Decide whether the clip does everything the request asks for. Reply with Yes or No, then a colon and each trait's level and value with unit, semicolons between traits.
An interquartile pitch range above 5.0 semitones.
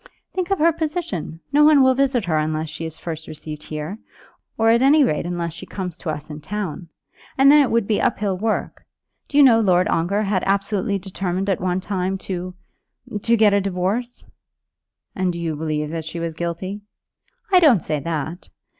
Yes: wide, 5.5 semitones